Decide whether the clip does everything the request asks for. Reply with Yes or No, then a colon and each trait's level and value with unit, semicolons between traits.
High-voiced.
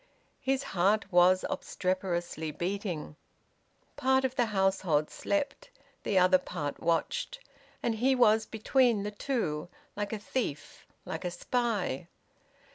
Yes: high, 200 Hz